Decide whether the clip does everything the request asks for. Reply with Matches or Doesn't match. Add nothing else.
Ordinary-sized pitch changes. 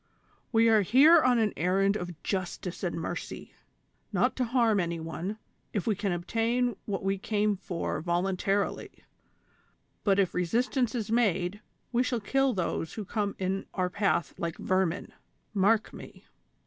Matches